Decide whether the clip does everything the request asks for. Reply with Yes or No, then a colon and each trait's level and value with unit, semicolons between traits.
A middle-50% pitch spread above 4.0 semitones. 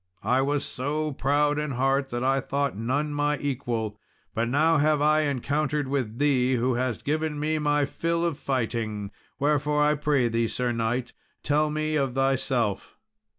No: average, 3.1 semitones